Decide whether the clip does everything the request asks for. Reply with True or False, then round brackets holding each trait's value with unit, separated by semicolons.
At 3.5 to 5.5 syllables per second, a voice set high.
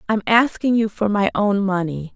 True (4.8 syllables/s; 205 Hz)